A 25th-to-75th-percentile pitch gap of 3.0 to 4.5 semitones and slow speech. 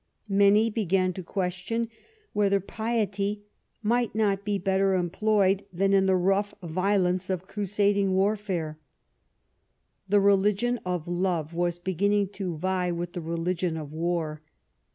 No: narrow, 2.5 semitones; slow, 130 wpm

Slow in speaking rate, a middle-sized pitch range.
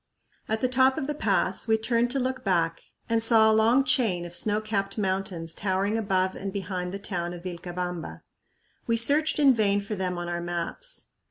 No: average, 195 wpm; average, 4.2 semitones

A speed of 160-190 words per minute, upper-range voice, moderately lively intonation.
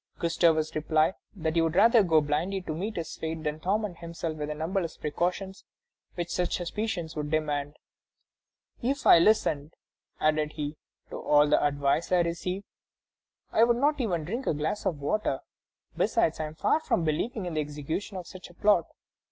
No: average, 175 wpm; medium, 165 Hz; average, 3.9 semitones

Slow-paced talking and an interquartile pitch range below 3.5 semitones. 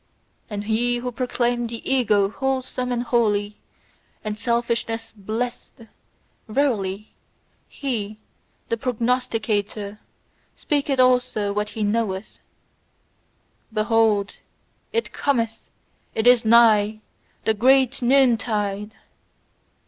Yes: slow, 90 wpm; average, 2.9 semitones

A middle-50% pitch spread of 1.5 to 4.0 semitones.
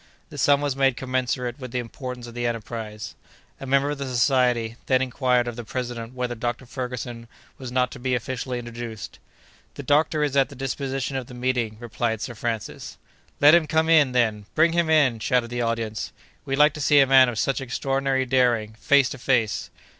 Yes: narrow, 2.4 semitones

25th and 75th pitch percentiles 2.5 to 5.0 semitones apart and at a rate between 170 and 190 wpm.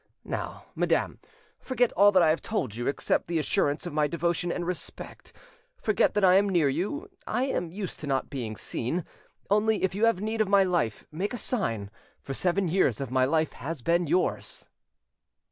No: wide, 5.6 semitones; average, 185 wpm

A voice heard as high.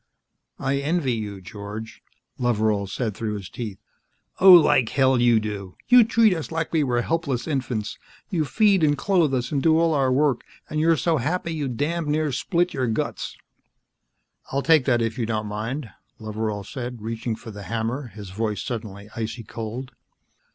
No: low, 125 Hz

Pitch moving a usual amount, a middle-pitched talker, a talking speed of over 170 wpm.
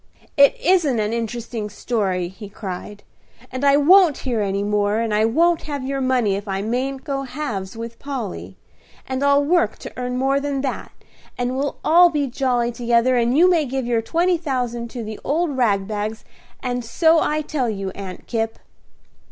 No: average, 4.5 semitones; high, 245 Hz; average, 185 wpm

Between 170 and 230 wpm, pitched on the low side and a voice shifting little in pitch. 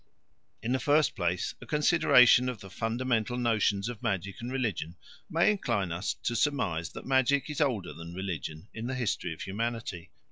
No: average, 175 wpm; low, 115 Hz; average, 5.2 semitones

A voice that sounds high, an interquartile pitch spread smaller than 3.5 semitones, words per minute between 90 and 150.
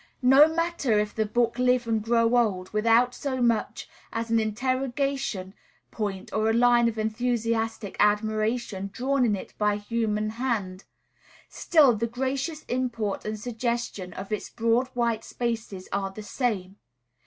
Yes: high, 230 Hz; narrow, 2.6 semitones; average, 145 wpm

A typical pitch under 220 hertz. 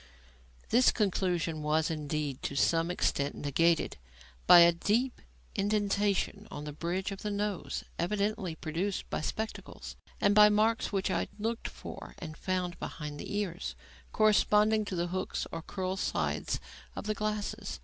Yes: high, 190 Hz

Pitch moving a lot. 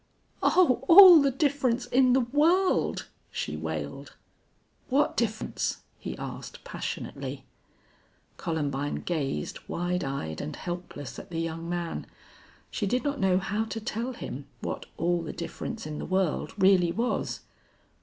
Yes: wide, 7.3 semitones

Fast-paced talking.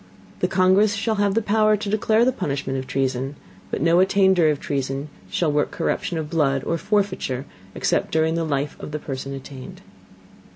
No: average, 175 wpm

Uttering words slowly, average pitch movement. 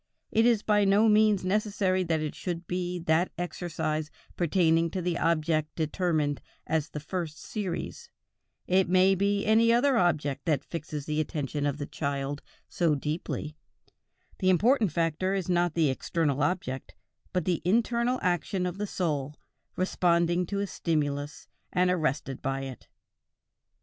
No: average, 150 wpm; average, 3.8 semitones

